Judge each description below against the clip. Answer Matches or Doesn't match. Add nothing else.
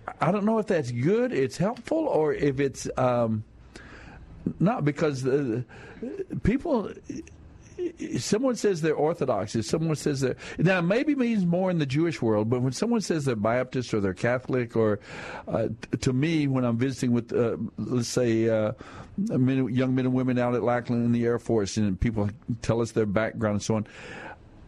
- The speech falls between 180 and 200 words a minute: Matches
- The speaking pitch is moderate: Doesn't match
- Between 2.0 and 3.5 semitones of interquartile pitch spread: Doesn't match